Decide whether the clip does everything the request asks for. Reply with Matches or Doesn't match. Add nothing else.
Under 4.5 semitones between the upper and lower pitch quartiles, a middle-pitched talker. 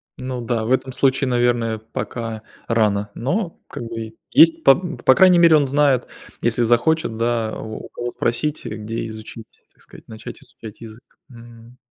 Doesn't match